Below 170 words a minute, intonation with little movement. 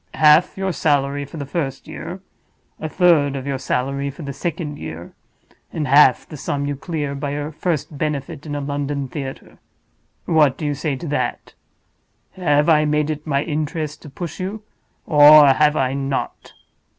No: average, 175 wpm; narrow, 2.0 semitones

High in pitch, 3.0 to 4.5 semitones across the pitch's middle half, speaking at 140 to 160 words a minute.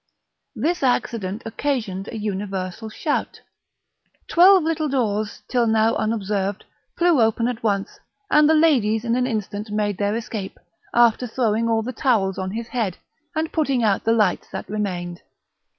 Yes: high, 225 Hz; average, 3.6 semitones; average, 150 wpm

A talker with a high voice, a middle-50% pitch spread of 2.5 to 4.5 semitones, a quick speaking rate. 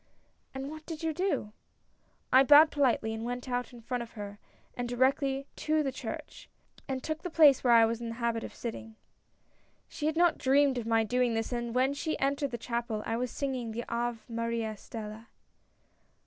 Yes: high, 245 Hz; average, 3.3 semitones; fast, 210 wpm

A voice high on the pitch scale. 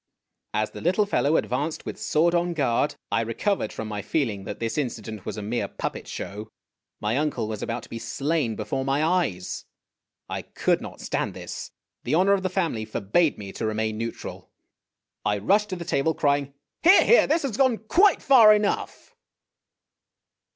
No: medium, 140 Hz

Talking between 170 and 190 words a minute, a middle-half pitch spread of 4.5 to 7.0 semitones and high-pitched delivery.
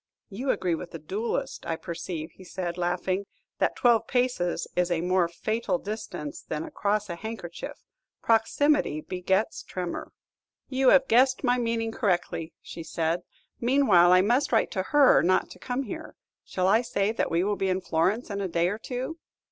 Yes: average, 175 wpm; average, 5.0 semitones; high, 195 Hz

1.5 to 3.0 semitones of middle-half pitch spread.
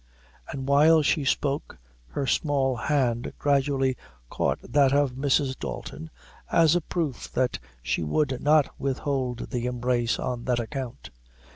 Yes: narrow, 2.6 semitones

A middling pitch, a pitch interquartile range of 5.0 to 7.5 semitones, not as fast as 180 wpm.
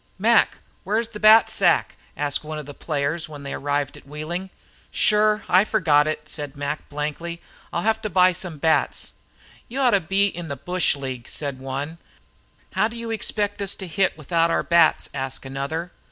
No: medium, 165 Hz; wide, 5.5 semitones; average, 185 wpm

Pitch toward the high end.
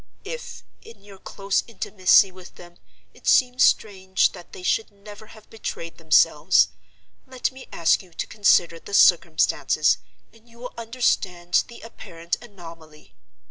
Yes: high, 200 Hz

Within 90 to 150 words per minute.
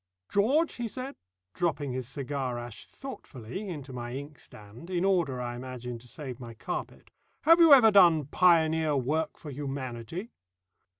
Yes: average, 145 wpm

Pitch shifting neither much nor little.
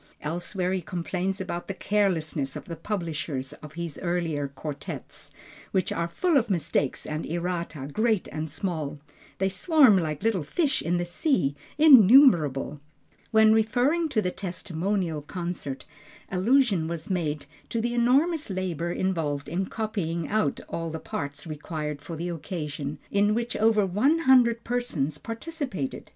No: wide, 5.8 semitones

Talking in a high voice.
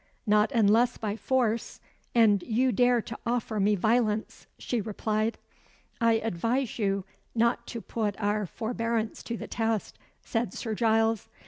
Yes: high, 225 Hz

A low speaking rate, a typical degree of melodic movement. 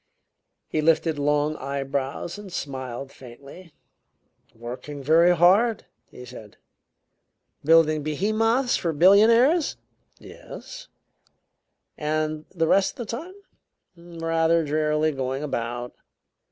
Yes: slow, 100 wpm; average, 4.6 semitones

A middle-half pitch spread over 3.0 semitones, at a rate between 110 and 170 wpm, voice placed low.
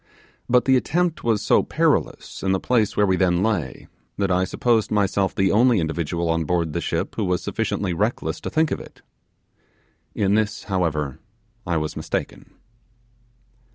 Yes: average, 4.2 semitones; average, 165 wpm; very low, 95 Hz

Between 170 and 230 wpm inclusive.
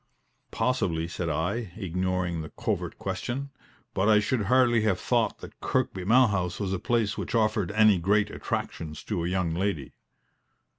No: average, 155 wpm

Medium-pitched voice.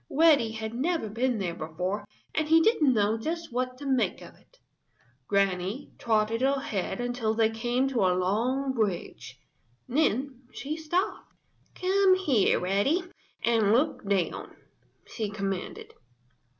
No: high, 235 Hz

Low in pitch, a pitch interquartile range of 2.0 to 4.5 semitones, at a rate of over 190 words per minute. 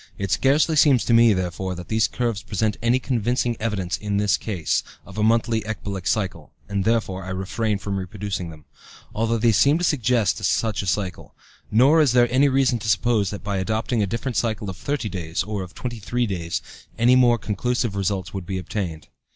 Yes: low, 105 Hz; average, 3.8 semitones; average, 200 wpm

